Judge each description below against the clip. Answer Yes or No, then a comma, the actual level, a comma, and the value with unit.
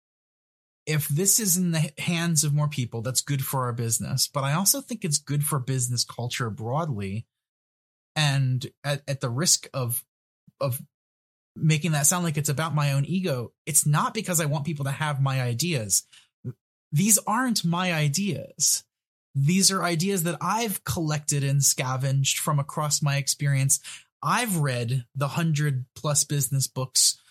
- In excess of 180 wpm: No, average, 160 wpm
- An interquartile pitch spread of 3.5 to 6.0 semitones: Yes, average, 4.2 semitones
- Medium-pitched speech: Yes, medium, 145 Hz